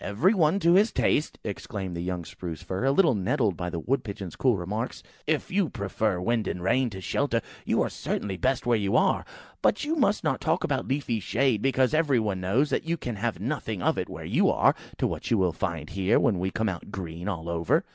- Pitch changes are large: Yes, wide, 6.7 semitones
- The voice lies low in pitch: Yes, low, 105 Hz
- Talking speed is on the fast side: Yes, fast, 230 wpm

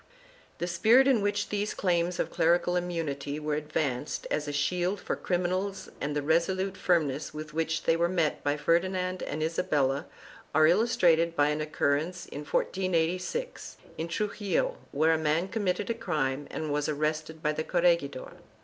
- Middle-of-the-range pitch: Yes, medium, 165 Hz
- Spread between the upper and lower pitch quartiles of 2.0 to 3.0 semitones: No, average, 3.5 semitones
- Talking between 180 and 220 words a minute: No, average, 170 wpm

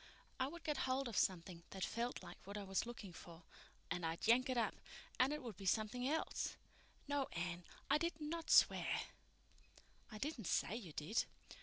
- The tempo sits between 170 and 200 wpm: Yes, average, 185 wpm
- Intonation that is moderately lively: No, wide, 6.6 semitones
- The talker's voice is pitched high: Yes, high, 230 Hz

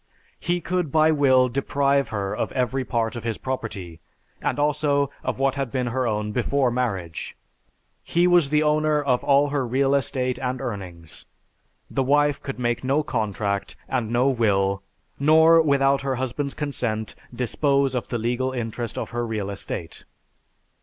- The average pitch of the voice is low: Yes, low, 130 Hz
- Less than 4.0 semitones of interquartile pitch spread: Yes, average, 3.6 semitones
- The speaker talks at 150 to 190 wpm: Yes, average, 160 wpm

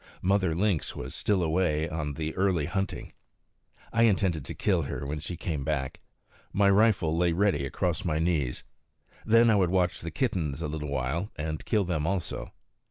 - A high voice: No, very low, 85 Hz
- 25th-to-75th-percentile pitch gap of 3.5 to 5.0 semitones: Yes, average, 4.1 semitones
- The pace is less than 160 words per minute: No, average, 175 wpm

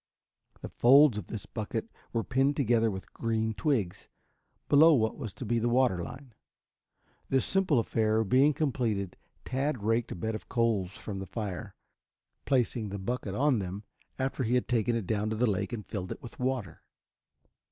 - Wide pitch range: No, average, 3.7 semitones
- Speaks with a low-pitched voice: Yes, low, 115 Hz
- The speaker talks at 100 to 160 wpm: No, average, 175 wpm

